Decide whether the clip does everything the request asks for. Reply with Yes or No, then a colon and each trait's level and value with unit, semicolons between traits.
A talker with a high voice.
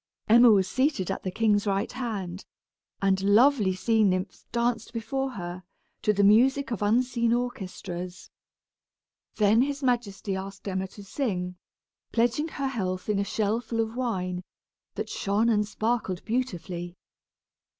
Yes: high, 210 Hz